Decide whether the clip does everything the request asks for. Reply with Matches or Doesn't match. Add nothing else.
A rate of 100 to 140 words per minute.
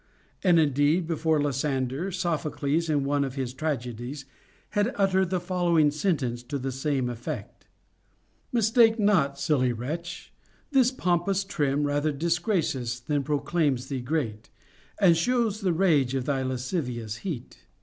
Matches